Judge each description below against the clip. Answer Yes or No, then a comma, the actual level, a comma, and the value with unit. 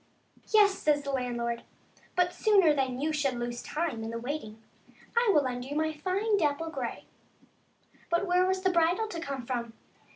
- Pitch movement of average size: No, wide, 6.4 semitones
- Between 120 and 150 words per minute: No, average, 185 wpm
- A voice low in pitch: No, very high, 300 Hz